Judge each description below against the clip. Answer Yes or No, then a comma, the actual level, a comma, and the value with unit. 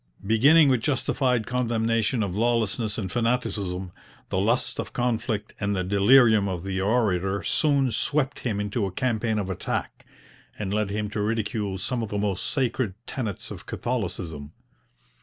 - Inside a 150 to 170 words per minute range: Yes, average, 155 wpm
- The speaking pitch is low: Yes, low, 110 Hz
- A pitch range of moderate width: Yes, average, 3.6 semitones